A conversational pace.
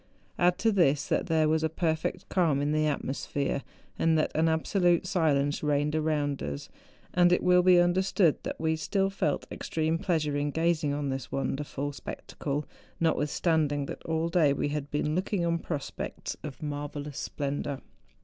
Yes: average, 170 wpm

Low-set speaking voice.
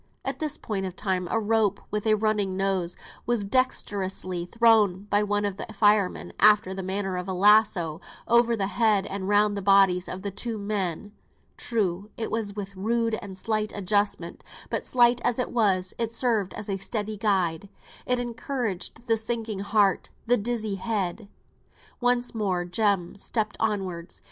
No: high, 205 Hz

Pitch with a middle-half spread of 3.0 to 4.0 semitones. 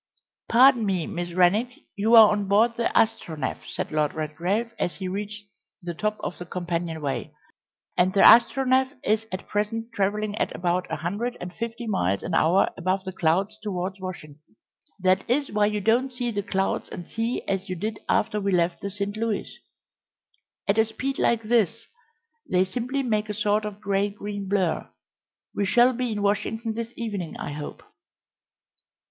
Yes: average, 3.6 semitones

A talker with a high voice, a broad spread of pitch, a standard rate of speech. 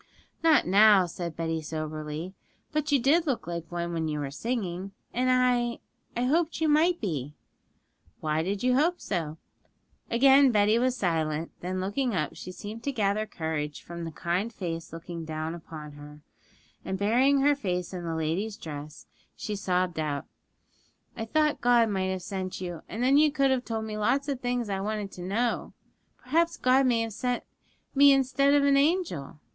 Yes: high, 205 Hz; wide, 7.3 semitones; average, 180 wpm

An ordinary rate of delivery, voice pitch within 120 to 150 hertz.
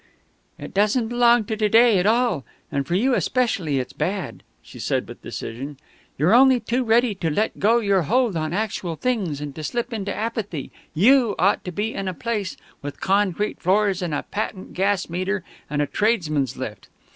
No: average, 190 wpm; high, 200 Hz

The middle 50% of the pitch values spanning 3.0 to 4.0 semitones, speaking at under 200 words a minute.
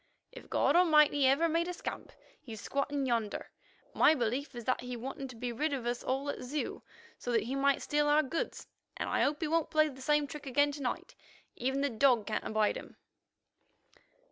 No: average, 3.3 semitones; fast, 205 wpm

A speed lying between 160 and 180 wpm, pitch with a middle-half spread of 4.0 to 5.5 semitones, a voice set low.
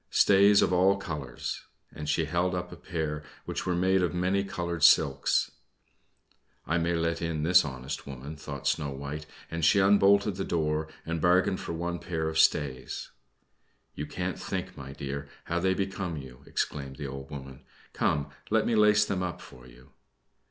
Yes: average, 175 wpm; average, 4.3 semitones; very low, 85 Hz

